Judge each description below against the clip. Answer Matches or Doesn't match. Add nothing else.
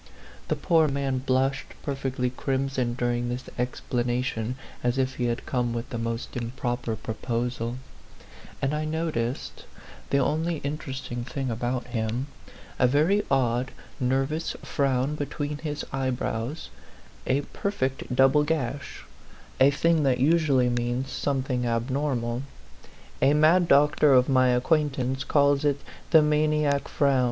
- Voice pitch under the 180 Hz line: Matches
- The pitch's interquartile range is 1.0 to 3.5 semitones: Matches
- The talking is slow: Matches